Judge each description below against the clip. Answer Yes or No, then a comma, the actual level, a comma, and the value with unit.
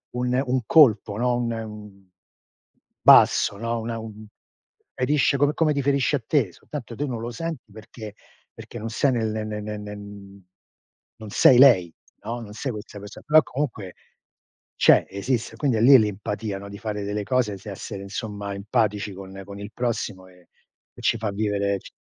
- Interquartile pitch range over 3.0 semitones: Yes, average, 3.4 semitones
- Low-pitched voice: Yes, low, 110 Hz